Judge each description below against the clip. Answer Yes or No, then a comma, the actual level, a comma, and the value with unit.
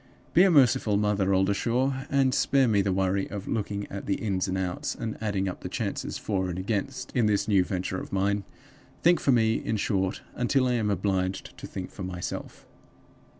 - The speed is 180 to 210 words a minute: Yes, average, 195 wpm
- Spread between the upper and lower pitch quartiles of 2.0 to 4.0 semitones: Yes, average, 3.7 semitones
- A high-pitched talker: No, low, 100 Hz